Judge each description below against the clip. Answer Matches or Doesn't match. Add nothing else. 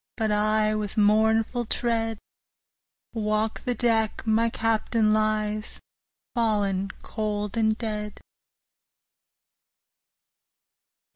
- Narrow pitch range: Matches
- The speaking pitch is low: Doesn't match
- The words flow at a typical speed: Doesn't match